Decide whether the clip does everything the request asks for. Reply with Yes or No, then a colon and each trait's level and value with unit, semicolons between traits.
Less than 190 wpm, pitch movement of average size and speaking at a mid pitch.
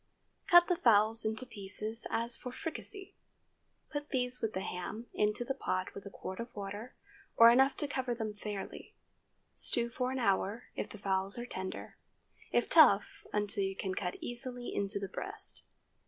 No: average, 170 wpm; average, 3.8 semitones; high, 225 Hz